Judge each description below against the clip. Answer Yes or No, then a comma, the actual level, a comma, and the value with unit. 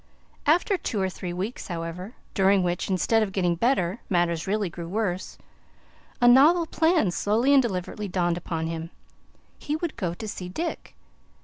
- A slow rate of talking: No, average, 165 wpm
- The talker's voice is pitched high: Yes, high, 195 Hz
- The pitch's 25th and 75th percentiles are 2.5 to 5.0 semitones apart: No, wide, 5.5 semitones